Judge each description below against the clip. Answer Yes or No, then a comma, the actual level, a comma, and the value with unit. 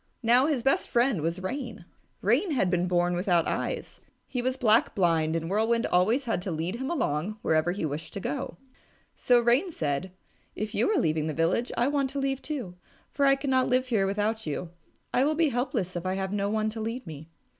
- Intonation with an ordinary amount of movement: No, wide, 6.5 semitones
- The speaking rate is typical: No, fast, 215 wpm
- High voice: Yes, high, 215 Hz